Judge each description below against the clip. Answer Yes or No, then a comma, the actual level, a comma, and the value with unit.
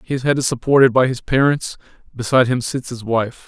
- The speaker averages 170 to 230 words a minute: Yes, fast, 205 wpm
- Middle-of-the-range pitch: No, low, 125 Hz